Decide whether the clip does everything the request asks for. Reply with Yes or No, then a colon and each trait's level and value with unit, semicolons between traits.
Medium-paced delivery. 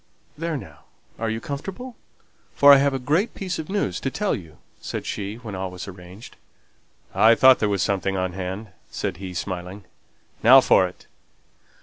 Yes: average, 180 wpm